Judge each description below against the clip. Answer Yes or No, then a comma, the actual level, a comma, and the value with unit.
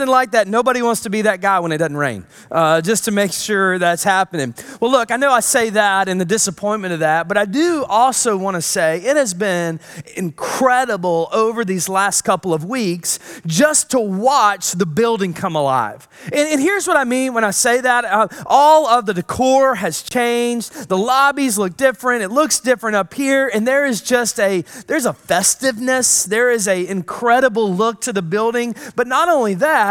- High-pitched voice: Yes, high, 220 Hz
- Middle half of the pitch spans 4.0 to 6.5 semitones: Yes, average, 5.2 semitones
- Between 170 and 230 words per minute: Yes, fast, 205 wpm